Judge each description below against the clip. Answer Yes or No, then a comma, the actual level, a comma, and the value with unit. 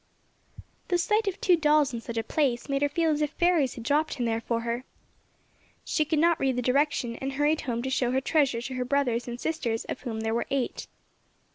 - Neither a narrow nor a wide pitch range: Yes, average, 4.2 semitones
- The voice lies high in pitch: Yes, very high, 270 Hz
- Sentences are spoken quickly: Yes, fast, 230 wpm